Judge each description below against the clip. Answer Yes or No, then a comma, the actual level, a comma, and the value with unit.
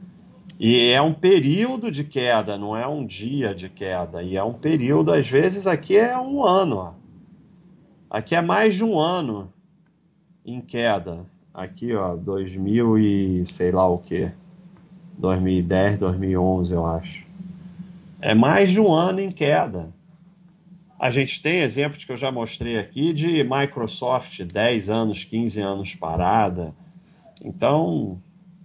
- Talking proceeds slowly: No, average, 140 wpm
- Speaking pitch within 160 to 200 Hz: No, medium, 140 Hz